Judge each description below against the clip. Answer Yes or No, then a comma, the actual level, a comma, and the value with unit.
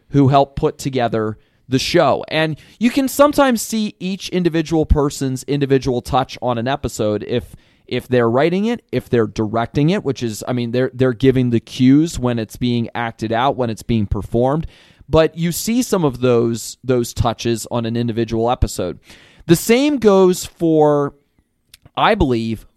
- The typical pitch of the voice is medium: No, low, 130 Hz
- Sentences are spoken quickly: No, average, 170 wpm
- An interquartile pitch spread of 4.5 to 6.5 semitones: Yes, average, 5.1 semitones